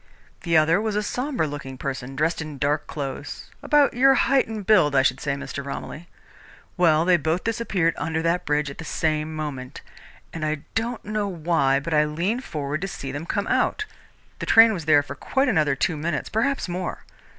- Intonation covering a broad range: Yes, wide, 5.7 semitones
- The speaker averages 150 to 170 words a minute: No, average, 195 wpm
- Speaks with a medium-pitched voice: Yes, medium, 160 Hz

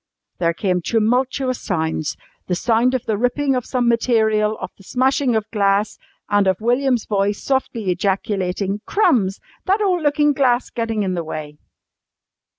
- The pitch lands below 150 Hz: No, high, 220 Hz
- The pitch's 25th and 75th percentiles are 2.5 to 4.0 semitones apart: No, average, 4.5 semitones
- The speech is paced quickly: No, average, 155 wpm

